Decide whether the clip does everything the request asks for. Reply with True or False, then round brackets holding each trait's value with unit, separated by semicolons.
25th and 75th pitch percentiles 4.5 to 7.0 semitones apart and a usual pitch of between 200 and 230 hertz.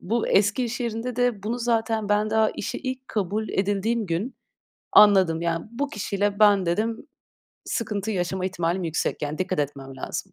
False (3.5 semitones; 205 Hz)